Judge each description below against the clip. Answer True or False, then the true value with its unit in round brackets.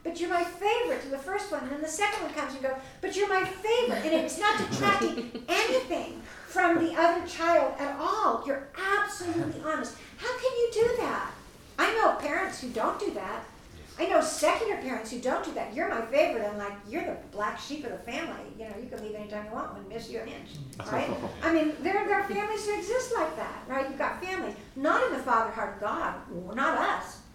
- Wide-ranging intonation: True (6.9 semitones)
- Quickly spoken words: True (225 wpm)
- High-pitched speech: True (330 Hz)